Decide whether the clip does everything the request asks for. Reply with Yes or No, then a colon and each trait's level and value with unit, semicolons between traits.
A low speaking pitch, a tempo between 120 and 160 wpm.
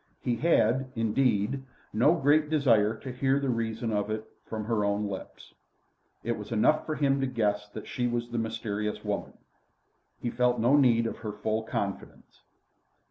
No: low, 115 Hz; average, 170 wpm